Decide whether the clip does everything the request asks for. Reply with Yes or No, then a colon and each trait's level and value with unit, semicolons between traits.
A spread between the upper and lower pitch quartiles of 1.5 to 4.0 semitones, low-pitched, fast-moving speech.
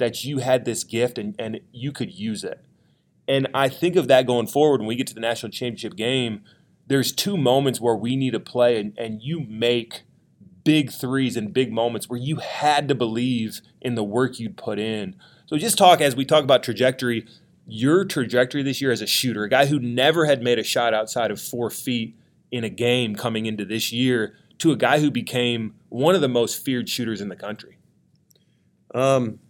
Yes: average, 2.9 semitones; low, 125 Hz; fast, 210 wpm